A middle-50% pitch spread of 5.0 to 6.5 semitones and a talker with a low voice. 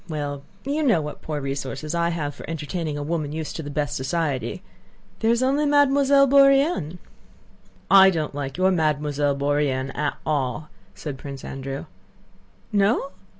No: wide, 5.5 semitones; medium, 155 Hz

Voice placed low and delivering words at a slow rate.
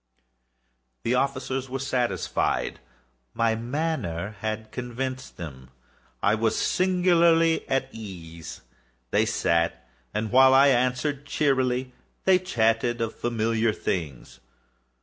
Yes: low, 120 Hz; slow, 105 wpm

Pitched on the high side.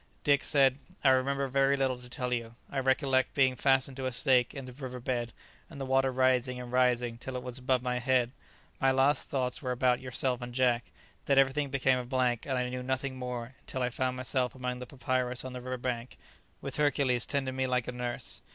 No: low, 130 Hz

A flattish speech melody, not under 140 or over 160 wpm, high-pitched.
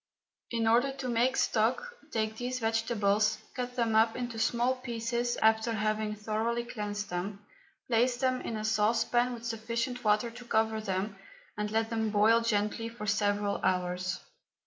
Yes: narrow, 2.1 semitones; average, 155 wpm; high, 225 Hz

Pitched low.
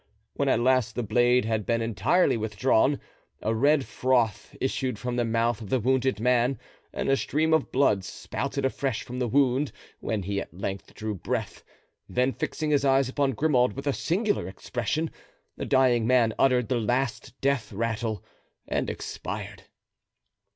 Yes: low, 125 Hz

